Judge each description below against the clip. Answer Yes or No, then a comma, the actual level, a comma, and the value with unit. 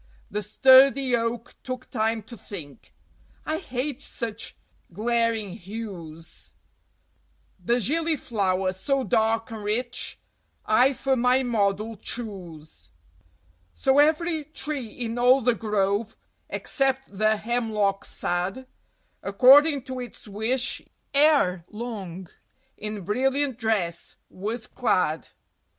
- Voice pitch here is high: Yes, high, 230 Hz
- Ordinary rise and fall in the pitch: Yes, average, 4.3 semitones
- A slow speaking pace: Yes, slow, 105 wpm